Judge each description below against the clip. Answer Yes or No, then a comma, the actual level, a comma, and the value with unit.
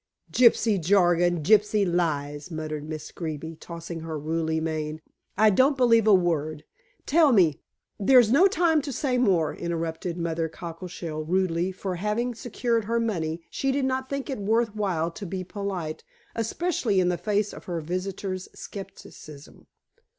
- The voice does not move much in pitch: No, wide, 5.5 semitones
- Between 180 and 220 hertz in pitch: Yes, medium, 185 Hz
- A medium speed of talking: Yes, average, 155 wpm